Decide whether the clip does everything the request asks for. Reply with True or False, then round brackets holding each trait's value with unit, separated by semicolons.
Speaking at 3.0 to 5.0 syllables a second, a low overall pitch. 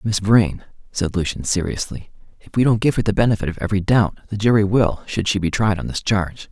False (6.0 syllables/s; 100 Hz)